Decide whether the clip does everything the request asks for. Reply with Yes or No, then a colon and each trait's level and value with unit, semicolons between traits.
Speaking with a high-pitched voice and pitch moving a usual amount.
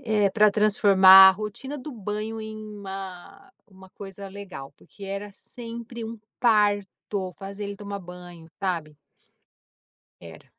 No: high, 200 Hz; narrow, 2.1 semitones